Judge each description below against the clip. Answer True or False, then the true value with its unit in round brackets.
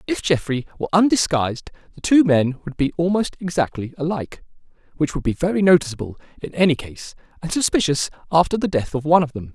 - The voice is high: False (160 Hz)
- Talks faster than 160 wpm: True (180 wpm)